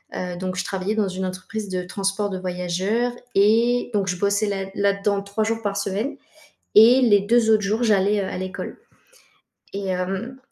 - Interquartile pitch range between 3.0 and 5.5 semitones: No, narrow, 2.5 semitones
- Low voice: No, high, 200 Hz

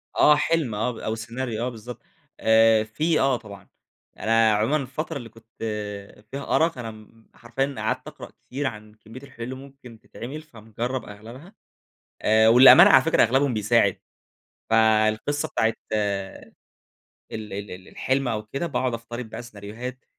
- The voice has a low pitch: Yes, low, 115 Hz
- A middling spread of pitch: Yes, average, 3.4 semitones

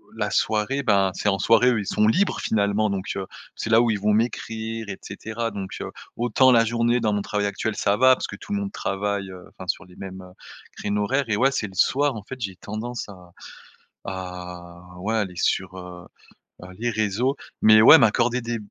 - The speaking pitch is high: No, low, 105 Hz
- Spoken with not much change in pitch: No, average, 3.3 semitones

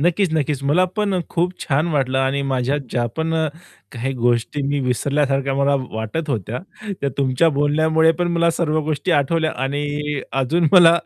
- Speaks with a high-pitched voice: No, medium, 145 Hz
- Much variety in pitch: No, average, 3.3 semitones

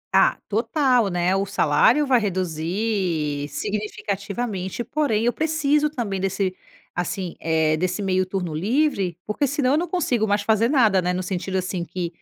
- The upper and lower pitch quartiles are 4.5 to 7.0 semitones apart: Yes, average, 5.1 semitones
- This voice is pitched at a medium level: No, high, 200 Hz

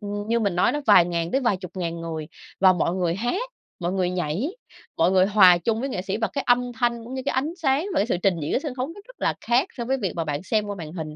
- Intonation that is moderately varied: No, wide, 6.0 semitones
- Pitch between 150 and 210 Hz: Yes, high, 205 Hz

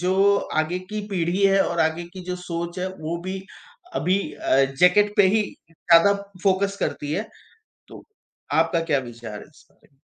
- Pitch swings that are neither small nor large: Yes, average, 3.0 semitones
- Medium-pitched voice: Yes, medium, 180 Hz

